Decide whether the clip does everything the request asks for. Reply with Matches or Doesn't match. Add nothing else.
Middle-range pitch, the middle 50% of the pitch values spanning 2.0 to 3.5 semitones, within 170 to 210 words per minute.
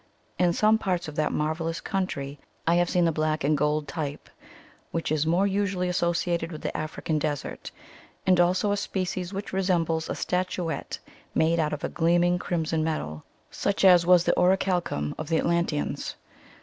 Matches